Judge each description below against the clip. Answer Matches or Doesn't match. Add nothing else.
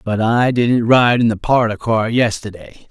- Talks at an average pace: Matches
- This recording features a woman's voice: Doesn't match